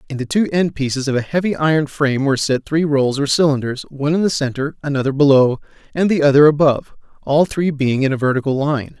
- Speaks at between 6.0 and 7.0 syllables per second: Yes, 6.2 syllables/s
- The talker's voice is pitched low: No, medium, 145 Hz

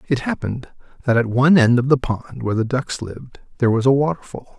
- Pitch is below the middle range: Yes, low, 130 Hz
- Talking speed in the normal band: No, fast, 220 wpm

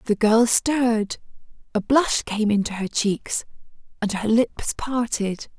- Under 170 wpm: Yes, average, 140 wpm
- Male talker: No, female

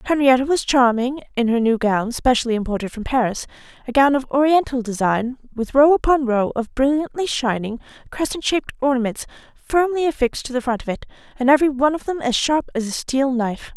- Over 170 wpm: Yes, average, 190 wpm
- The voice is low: No, very high, 260 Hz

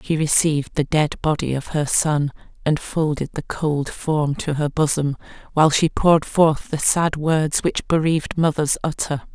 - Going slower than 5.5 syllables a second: Yes, 4.5 syllables/s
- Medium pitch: Yes, medium, 155 Hz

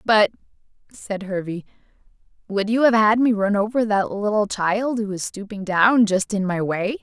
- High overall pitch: Yes, high, 205 Hz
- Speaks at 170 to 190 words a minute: Yes, average, 180 wpm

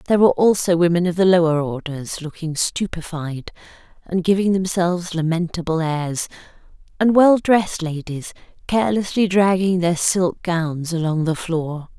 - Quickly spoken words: No, slow, 135 wpm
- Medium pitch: Yes, medium, 175 Hz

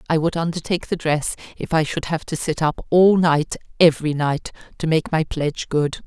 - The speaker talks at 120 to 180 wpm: No, average, 200 wpm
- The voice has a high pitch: No, medium, 160 Hz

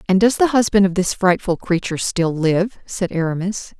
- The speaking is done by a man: No, female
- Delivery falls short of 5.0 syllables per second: No, 5.1 syllables/s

